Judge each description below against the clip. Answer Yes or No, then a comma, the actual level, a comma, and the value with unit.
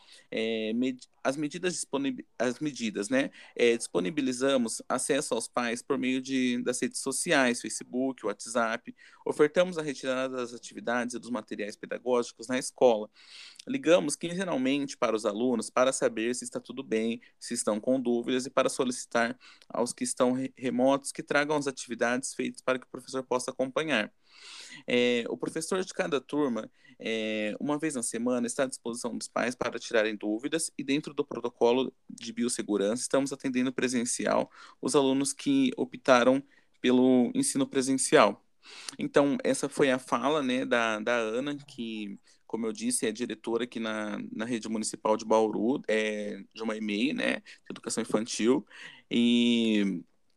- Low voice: Yes, low, 125 Hz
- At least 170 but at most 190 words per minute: No, average, 155 wpm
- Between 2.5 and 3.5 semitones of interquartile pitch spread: Yes, average, 2.9 semitones